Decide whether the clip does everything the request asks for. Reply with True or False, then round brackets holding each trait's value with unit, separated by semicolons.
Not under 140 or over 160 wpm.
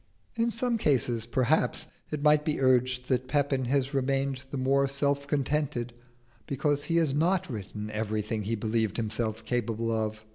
True (155 wpm)